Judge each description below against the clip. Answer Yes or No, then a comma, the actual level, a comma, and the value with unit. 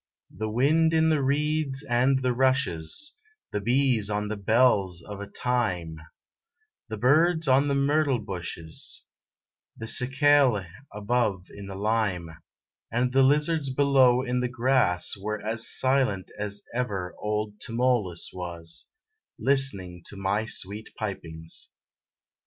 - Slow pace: Yes, slow, 125 wpm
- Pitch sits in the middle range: No, low, 115 Hz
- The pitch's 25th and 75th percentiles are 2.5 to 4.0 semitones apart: No, average, 5.2 semitones